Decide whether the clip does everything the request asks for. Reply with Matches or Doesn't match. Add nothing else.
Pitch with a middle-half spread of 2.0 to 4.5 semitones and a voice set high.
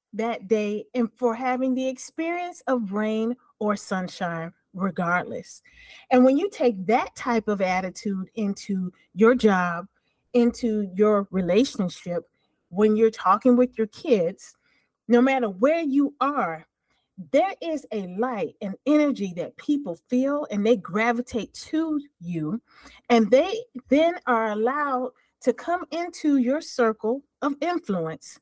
Doesn't match